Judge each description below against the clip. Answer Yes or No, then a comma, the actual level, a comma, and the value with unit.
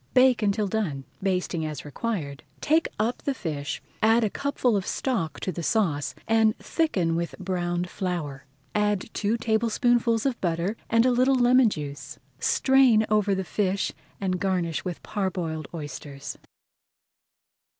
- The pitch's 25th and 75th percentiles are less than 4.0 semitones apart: No, wide, 5.4 semitones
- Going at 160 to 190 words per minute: No, average, 140 wpm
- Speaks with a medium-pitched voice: No, high, 200 Hz